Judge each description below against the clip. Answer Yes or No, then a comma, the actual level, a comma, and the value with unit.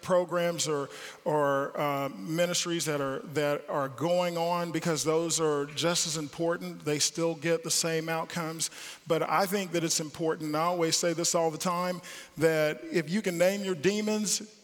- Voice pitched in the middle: Yes, medium, 165 Hz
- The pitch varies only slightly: Yes, narrow, 2.0 semitones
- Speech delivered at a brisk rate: No, average, 180 wpm